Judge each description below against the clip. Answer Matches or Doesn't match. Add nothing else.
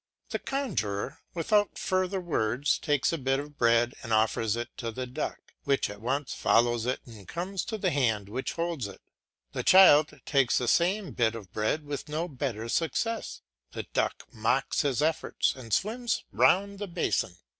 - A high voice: Doesn't match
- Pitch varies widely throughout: Matches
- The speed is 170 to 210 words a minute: Matches